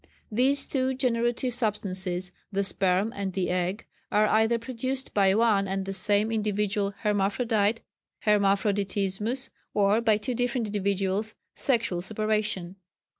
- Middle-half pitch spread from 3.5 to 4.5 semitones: No, average, 2.9 semitones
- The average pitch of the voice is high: Yes, high, 210 Hz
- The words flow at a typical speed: No, slow, 125 wpm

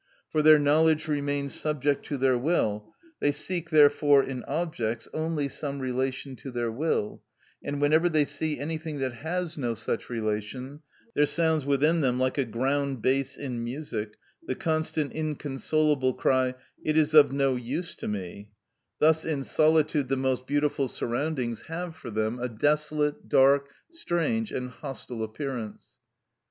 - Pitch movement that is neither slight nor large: Yes, average, 3.4 semitones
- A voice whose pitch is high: No, medium, 140 Hz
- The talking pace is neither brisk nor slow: Yes, average, 150 wpm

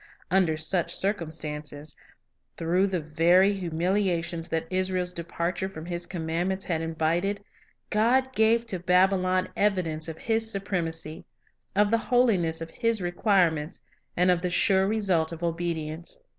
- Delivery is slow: Yes, slow, 130 wpm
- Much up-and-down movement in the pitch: No, average, 3.2 semitones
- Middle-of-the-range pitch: Yes, medium, 180 Hz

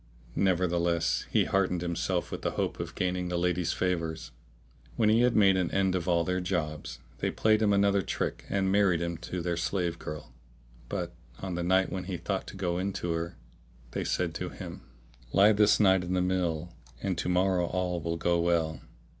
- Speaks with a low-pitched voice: Yes, very low, 90 Hz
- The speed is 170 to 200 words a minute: Yes, average, 195 wpm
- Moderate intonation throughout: No, narrow, 1.9 semitones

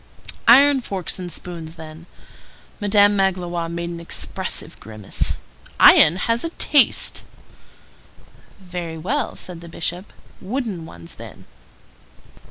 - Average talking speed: No, slow, 110 wpm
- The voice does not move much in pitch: No, average, 3.6 semitones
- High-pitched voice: No, medium, 180 Hz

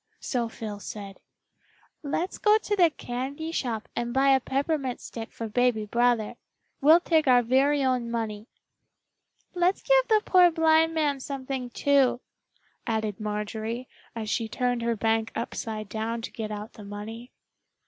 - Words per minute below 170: Yes, average, 150 wpm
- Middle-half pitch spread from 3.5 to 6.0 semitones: Yes, average, 4.4 semitones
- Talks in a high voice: Yes, high, 245 Hz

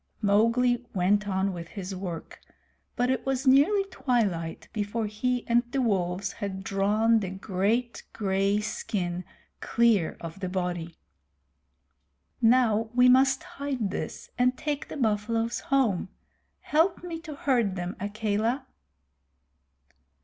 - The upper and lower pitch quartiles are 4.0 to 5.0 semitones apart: Yes, average, 4.6 semitones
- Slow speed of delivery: Yes, slow, 125 wpm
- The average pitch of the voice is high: Yes, high, 215 Hz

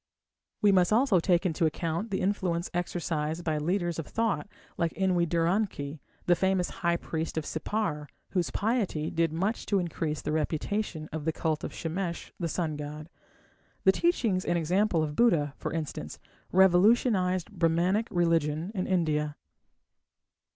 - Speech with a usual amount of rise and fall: Yes, average, 3.3 semitones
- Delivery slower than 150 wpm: No, average, 160 wpm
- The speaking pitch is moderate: Yes, medium, 175 Hz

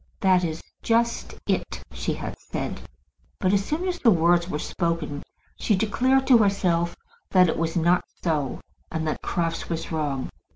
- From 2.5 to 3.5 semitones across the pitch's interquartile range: No, average, 3.9 semitones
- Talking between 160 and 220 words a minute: Yes, average, 165 wpm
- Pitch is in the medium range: Yes, medium, 175 Hz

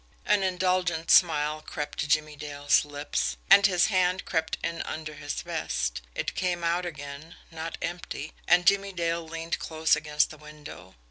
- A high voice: No, medium, 160 Hz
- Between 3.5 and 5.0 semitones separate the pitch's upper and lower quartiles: No, average, 3.0 semitones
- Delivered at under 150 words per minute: No, average, 160 wpm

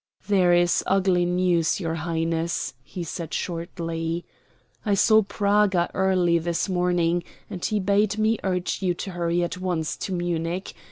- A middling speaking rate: Yes, average, 150 wpm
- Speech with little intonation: Yes, narrow, 2.1 semitones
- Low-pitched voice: No, medium, 175 Hz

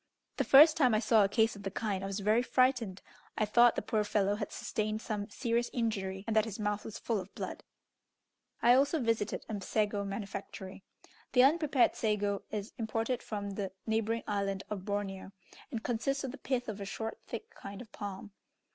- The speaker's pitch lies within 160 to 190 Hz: No, high, 215 Hz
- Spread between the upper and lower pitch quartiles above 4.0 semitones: No, average, 2.8 semitones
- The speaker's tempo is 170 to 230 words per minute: Yes, average, 195 wpm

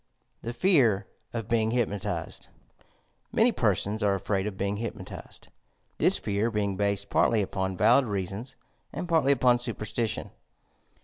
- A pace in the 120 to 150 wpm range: Yes, slow, 135 wpm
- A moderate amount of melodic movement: Yes, average, 3.0 semitones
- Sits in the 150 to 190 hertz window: No, low, 105 Hz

